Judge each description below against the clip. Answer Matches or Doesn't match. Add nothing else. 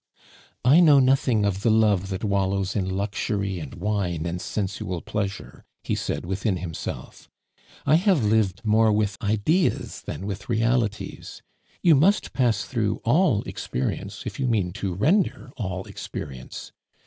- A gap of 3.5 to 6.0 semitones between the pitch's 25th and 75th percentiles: Matches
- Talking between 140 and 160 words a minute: Matches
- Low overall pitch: Matches